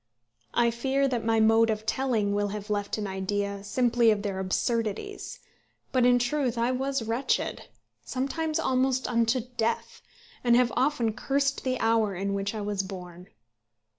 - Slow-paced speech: No, average, 160 wpm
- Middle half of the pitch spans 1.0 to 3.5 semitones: No, average, 3.9 semitones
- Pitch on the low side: No, high, 230 Hz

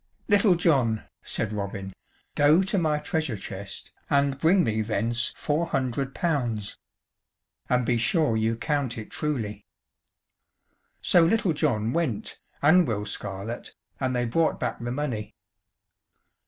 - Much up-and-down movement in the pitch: Yes, wide, 6.2 semitones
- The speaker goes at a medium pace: No, slow, 130 wpm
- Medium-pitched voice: No, low, 130 Hz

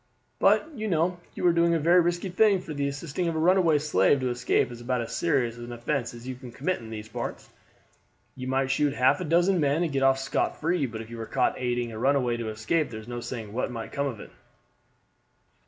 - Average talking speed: No, fast, 240 wpm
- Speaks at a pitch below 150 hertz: Yes, low, 135 Hz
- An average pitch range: No, wide, 5.8 semitones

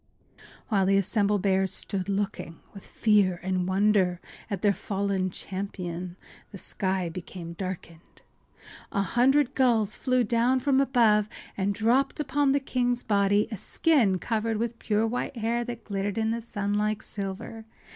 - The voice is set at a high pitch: Yes, high, 205 Hz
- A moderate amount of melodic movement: Yes, average, 3.5 semitones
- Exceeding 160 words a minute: No, average, 150 wpm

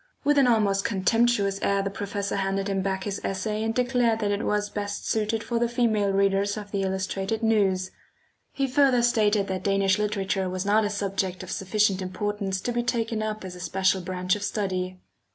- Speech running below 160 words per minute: No, average, 195 wpm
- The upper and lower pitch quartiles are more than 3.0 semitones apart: No, narrow, 2.4 semitones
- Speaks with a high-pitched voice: Yes, high, 205 Hz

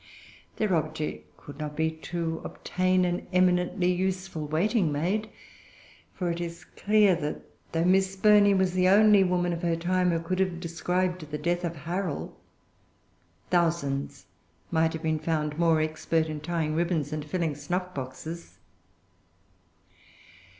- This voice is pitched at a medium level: Yes, medium, 170 Hz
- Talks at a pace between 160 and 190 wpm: No, average, 145 wpm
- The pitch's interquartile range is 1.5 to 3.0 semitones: Yes, narrow, 2.6 semitones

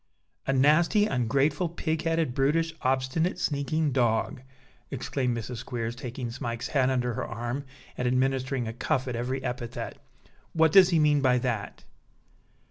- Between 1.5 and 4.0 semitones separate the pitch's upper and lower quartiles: Yes, average, 3.6 semitones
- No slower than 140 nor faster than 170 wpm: Yes, average, 145 wpm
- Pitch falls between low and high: No, low, 130 Hz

